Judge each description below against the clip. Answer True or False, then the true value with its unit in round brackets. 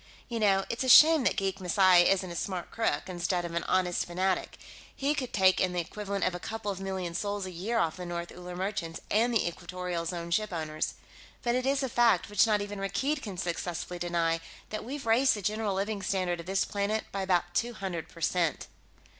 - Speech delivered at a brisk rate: True (215 wpm)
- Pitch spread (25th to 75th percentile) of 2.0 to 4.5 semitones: True (3.5 semitones)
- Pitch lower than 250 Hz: True (190 Hz)